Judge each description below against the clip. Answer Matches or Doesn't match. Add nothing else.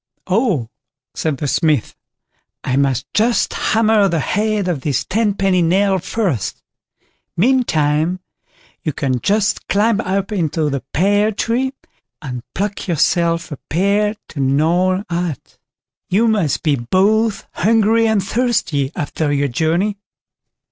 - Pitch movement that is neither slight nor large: Doesn't match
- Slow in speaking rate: Matches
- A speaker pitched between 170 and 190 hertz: Matches